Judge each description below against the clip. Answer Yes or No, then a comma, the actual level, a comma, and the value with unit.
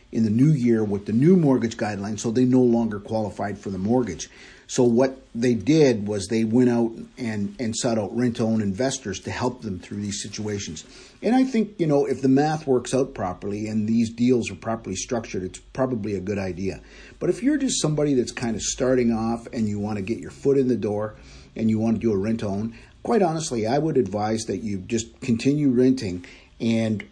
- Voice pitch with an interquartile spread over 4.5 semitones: No, average, 3.5 semitones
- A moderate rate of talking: No, fast, 215 wpm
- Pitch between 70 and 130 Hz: Yes, low, 115 Hz